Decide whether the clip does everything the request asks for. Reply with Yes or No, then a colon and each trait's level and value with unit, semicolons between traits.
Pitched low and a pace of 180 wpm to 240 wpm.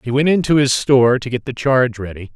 No: low, 125 Hz; fast, 255 wpm